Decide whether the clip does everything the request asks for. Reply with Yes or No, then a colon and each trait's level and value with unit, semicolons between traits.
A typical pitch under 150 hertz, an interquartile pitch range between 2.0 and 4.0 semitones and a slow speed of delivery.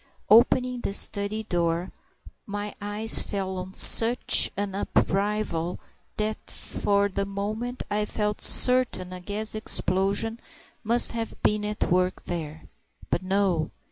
No: high, 205 Hz; narrow, 2.5 semitones; slow, 125 wpm